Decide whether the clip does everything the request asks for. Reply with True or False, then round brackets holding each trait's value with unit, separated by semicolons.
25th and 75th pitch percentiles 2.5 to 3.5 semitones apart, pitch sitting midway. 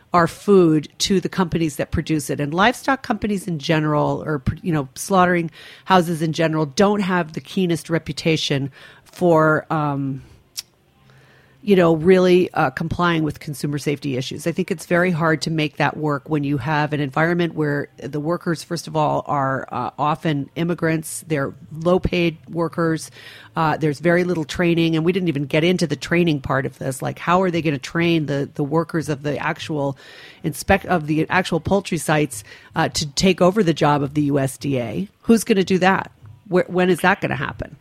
True (3.1 semitones; 160 Hz)